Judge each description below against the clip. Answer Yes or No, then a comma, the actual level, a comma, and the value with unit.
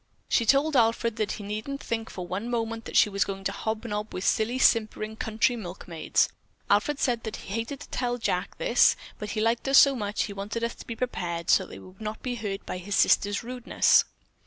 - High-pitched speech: Yes, high, 220 Hz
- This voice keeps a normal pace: No, fast, 225 wpm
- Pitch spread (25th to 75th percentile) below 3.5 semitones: Yes, average, 2.9 semitones